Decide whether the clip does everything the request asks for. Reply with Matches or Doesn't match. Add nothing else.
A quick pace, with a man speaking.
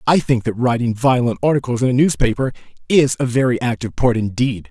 Doesn't match